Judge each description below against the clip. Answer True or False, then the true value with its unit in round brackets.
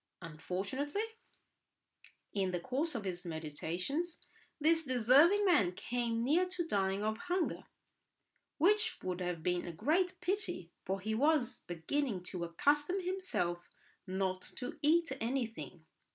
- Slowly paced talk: True (125 wpm)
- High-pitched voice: True (235 Hz)